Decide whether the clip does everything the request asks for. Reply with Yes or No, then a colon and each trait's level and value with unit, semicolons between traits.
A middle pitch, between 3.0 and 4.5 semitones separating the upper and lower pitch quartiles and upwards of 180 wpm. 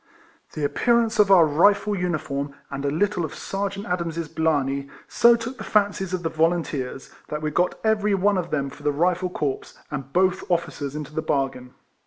No: medium, 170 Hz; average, 5.3 semitones; average, 190 wpm